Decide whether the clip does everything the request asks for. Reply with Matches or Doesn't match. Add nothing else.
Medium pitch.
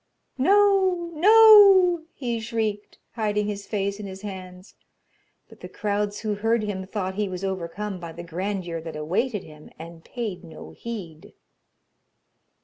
Doesn't match